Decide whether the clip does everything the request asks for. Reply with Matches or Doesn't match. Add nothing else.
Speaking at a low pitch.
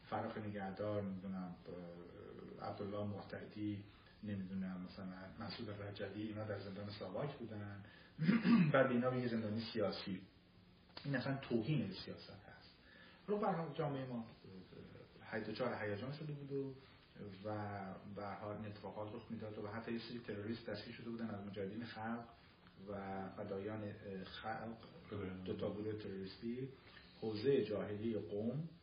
Matches